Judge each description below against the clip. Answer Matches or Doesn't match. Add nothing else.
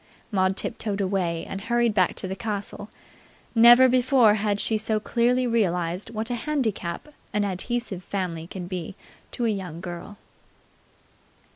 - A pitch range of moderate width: Matches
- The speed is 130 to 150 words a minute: Matches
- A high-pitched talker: Matches